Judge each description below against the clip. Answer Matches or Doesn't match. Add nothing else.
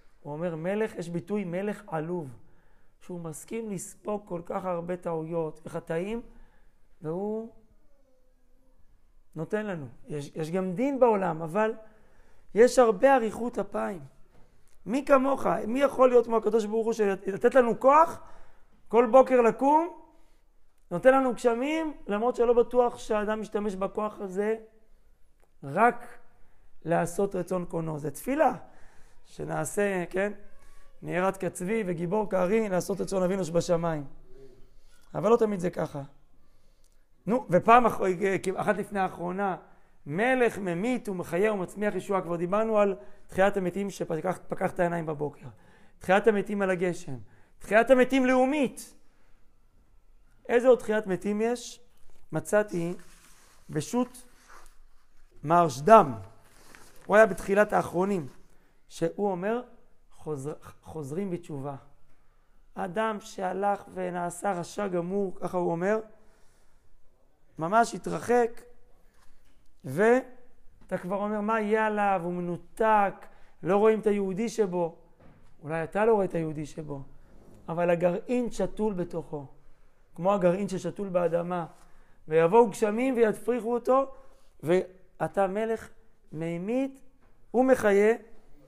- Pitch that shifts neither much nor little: Matches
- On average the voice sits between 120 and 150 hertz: Doesn't match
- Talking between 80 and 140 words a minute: Matches